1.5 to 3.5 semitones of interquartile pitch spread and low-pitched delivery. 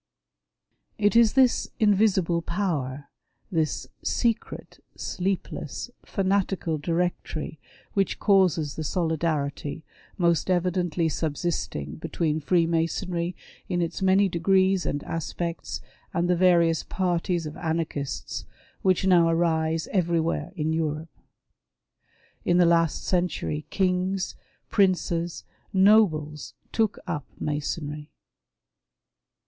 No: average, 2.9 semitones; medium, 170 Hz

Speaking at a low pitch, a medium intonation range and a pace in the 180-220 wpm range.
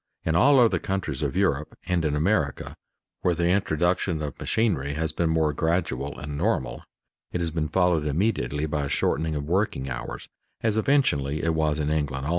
Yes: very low, 80 Hz; average, 3.7 semitones; average, 185 wpm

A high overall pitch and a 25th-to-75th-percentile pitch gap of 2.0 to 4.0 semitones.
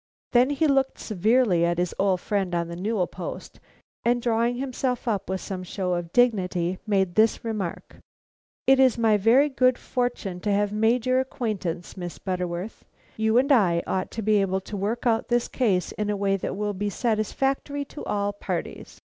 No: high, 210 Hz; average, 4.6 semitones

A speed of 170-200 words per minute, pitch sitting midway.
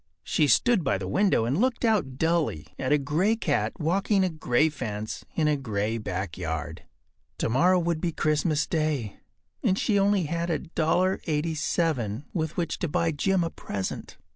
No: average, 160 wpm; medium, 155 Hz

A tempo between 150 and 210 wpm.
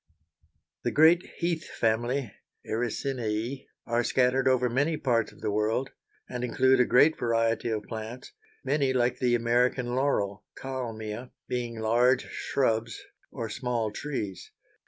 No: slow, 135 wpm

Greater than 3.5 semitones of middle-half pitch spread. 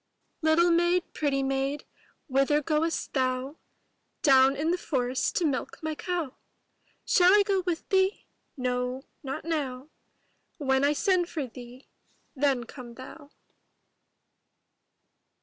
Yes: average, 4.2 semitones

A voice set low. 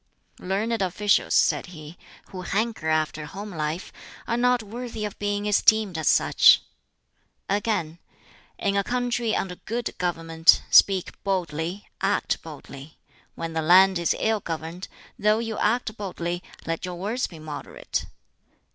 No: high, 190 Hz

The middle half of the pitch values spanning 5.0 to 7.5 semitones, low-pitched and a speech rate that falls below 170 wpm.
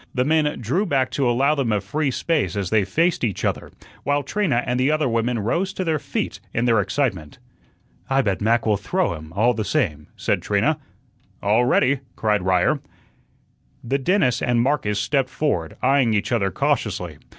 No: wide, 5.4 semitones; low, 125 Hz; average, 185 wpm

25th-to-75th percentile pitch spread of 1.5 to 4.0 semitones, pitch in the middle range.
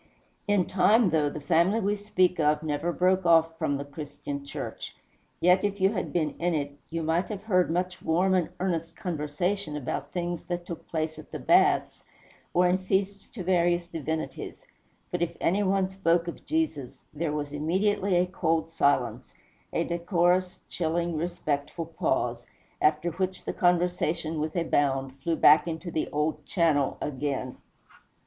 Yes: average, 3.1 semitones; medium, 170 Hz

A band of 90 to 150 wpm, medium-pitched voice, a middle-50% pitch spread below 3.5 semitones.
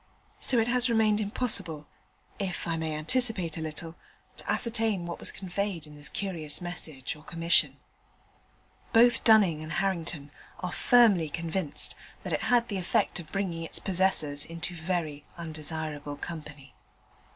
No: average, 145 wpm; medium, 170 Hz; average, 4.3 semitones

